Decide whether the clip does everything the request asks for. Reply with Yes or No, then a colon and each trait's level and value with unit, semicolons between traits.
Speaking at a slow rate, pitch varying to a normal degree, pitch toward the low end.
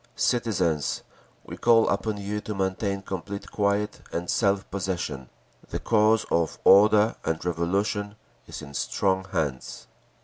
Yes: slow, 130 wpm; average, 3.4 semitones; low, 100 Hz